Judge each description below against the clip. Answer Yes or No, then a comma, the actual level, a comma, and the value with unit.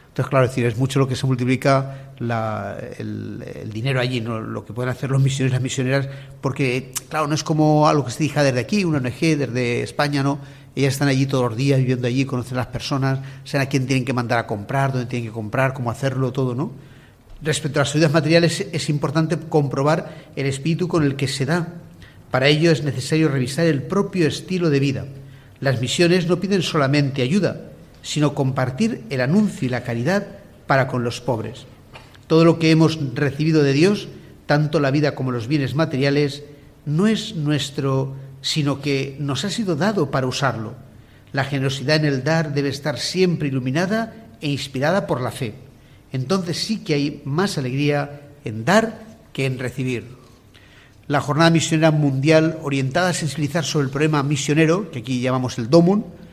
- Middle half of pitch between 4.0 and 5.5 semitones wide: No, average, 3.4 semitones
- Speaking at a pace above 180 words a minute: Yes, fast, 190 wpm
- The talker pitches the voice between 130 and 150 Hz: Yes, medium, 140 Hz